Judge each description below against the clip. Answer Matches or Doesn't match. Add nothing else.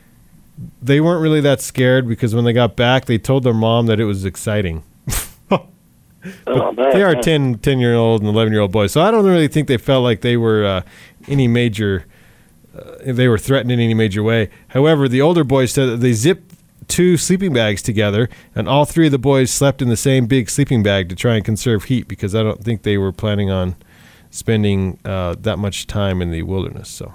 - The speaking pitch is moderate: Doesn't match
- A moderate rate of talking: Doesn't match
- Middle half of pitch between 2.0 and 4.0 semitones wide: Doesn't match